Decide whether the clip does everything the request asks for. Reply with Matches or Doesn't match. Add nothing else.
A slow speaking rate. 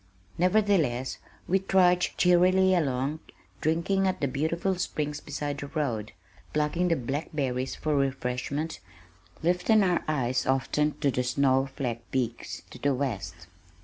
Matches